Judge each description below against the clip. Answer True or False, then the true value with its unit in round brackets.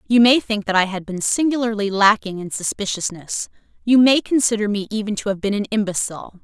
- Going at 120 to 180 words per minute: False (195 wpm)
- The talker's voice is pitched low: False (210 Hz)